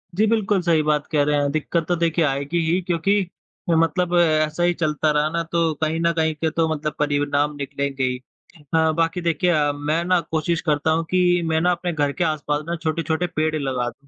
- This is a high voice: No, medium, 160 Hz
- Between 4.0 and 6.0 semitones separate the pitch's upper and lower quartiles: No, narrow, 2.4 semitones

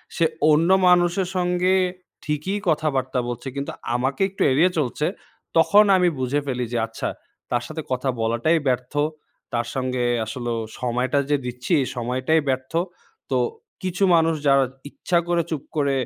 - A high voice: No, medium, 140 Hz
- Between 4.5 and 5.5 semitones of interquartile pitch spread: Yes, average, 4.8 semitones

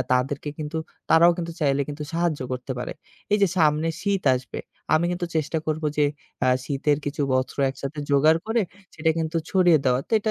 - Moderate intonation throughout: Yes, average, 3.2 semitones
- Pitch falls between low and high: Yes, medium, 155 Hz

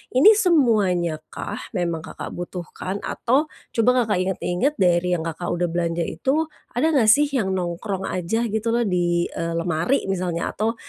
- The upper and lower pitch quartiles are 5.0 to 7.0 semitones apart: Yes, wide, 5.4 semitones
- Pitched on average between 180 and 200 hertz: Yes, high, 190 Hz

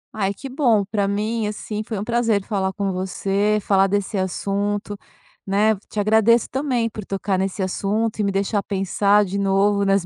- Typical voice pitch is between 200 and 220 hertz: Yes, high, 205 Hz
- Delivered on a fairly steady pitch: Yes, narrow, 1.7 semitones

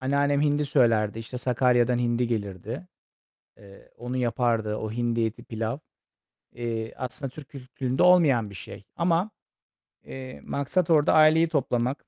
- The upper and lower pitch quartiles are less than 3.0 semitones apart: No, average, 3.7 semitones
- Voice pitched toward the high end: No, low, 125 Hz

